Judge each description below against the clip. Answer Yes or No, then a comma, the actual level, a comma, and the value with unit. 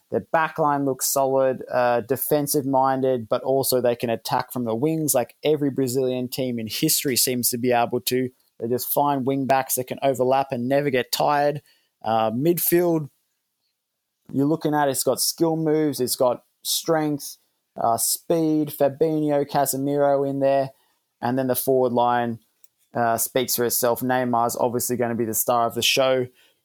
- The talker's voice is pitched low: Yes, low, 130 Hz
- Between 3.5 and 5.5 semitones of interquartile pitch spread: No, average, 2.7 semitones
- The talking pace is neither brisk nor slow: Yes, average, 170 wpm